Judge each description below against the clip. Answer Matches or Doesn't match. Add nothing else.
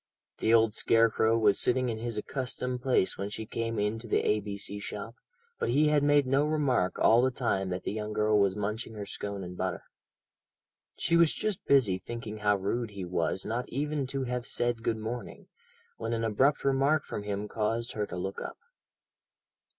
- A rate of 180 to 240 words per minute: Matches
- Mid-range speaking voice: Doesn't match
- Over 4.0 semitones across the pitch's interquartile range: Doesn't match